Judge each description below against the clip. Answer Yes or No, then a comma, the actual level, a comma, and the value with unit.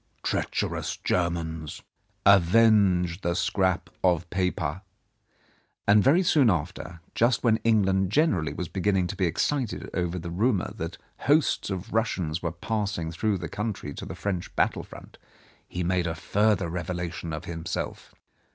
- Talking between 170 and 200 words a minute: No, average, 140 wpm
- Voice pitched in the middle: No, very low, 90 Hz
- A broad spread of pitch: No, average, 3.7 semitones